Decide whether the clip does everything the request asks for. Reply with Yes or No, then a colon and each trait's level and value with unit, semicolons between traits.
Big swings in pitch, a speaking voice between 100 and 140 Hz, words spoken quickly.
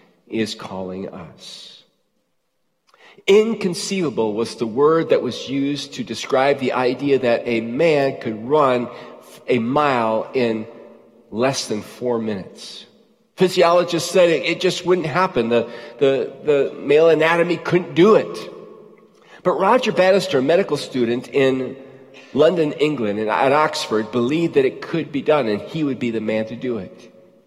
No: wide, 6.2 semitones; low, 135 Hz; average, 145 wpm